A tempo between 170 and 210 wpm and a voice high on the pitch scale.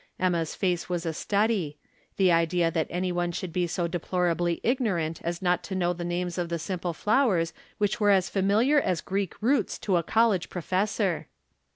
No: average, 185 wpm; medium, 180 Hz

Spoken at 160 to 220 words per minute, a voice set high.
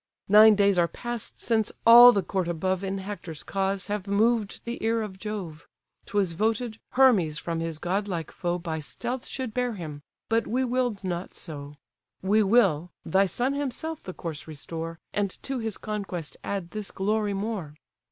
Yes: average, 170 wpm; high, 200 Hz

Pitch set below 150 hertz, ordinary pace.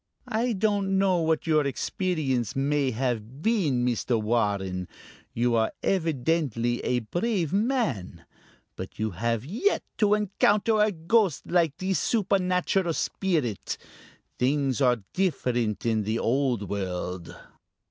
No: medium, 140 Hz; slow, 120 wpm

